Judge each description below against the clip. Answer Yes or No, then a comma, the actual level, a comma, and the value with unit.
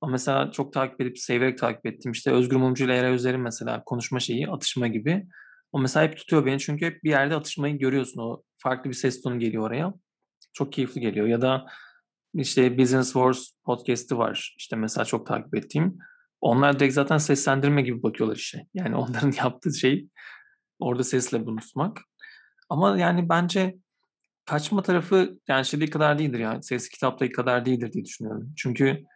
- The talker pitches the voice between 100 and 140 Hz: Yes, low, 135 Hz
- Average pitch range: Yes, average, 3.5 semitones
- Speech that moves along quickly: Yes, fast, 175 wpm